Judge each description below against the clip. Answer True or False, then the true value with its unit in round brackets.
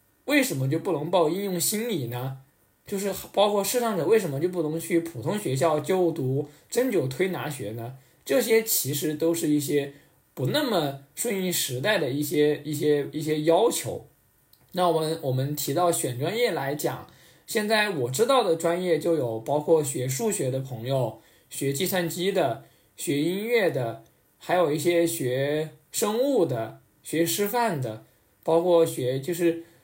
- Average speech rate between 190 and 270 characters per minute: True (235 characters per minute)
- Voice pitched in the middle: True (165 Hz)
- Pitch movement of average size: True (4.7 semitones)